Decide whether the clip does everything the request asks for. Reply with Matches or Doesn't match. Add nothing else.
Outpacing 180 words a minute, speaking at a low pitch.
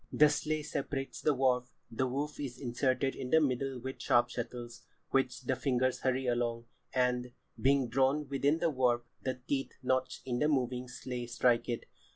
Doesn't match